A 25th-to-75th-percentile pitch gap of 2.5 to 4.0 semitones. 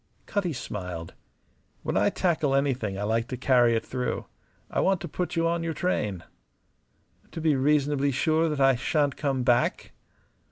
No: average, 4.8 semitones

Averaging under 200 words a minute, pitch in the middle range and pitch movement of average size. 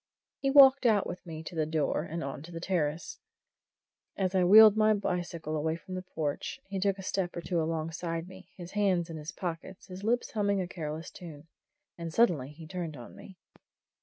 No: fast, 205 wpm; medium, 175 Hz; average, 3.2 semitones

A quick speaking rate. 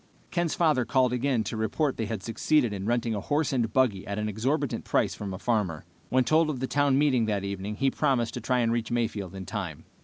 Yes: fast, 235 wpm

